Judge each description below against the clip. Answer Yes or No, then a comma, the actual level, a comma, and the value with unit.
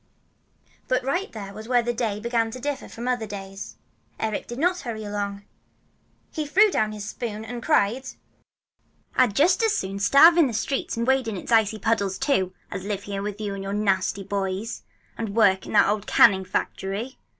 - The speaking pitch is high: Yes, high, 220 Hz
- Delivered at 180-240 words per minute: Yes, average, 195 wpm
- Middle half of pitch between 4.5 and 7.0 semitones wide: No, average, 4.1 semitones